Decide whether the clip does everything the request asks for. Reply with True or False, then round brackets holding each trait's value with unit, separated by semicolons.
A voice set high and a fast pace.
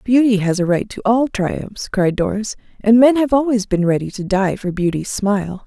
True (210 Hz; 210 wpm)